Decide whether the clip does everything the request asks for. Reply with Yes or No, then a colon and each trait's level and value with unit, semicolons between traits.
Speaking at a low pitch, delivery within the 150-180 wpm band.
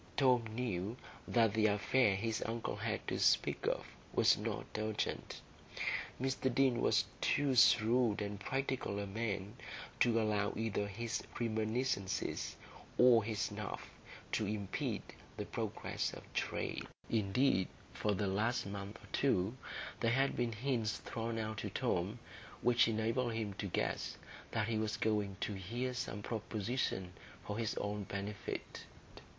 No: low, 110 Hz; average, 140 wpm